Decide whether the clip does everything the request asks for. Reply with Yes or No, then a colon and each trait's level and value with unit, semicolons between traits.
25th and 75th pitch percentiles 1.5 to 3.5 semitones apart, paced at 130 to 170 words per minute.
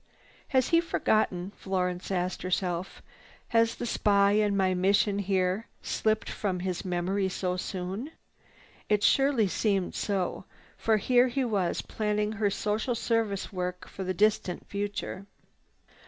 Yes: average, 2.8 semitones; slow, 135 wpm